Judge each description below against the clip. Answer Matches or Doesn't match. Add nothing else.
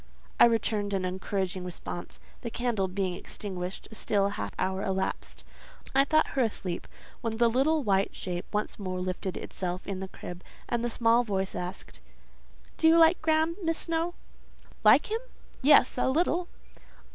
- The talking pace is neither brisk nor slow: Matches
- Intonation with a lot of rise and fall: Matches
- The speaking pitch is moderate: Doesn't match